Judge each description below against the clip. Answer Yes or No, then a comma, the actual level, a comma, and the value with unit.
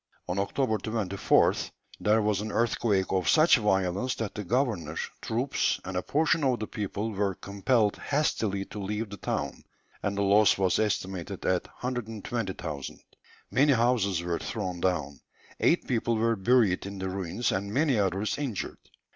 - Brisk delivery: No, average, 155 wpm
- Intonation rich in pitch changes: No, average, 3.5 semitones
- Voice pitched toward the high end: No, low, 105 Hz